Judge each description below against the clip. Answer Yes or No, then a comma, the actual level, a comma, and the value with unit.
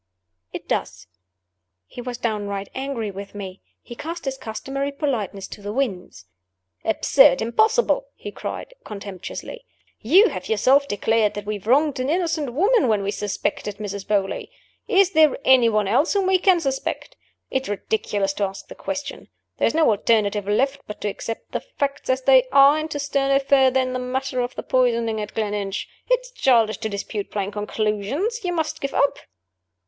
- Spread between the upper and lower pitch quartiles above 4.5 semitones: Yes, average, 5.3 semitones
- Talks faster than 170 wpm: Yes, average, 180 wpm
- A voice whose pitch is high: Yes, very high, 250 Hz